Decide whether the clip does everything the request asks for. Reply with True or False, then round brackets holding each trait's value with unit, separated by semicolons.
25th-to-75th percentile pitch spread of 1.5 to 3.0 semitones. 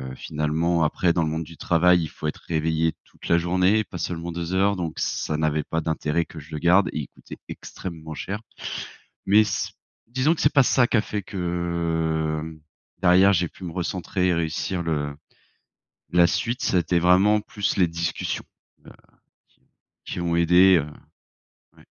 True (2.5 semitones)